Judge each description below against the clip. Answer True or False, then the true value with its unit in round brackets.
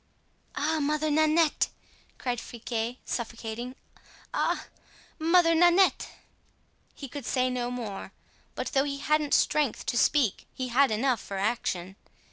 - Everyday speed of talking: False (125 wpm)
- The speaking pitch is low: False (260 Hz)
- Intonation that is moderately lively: True (4.5 semitones)